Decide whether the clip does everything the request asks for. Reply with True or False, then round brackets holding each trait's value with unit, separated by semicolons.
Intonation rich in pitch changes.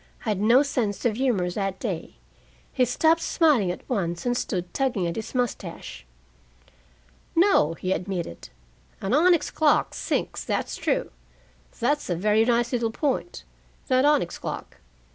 True (6.2 semitones)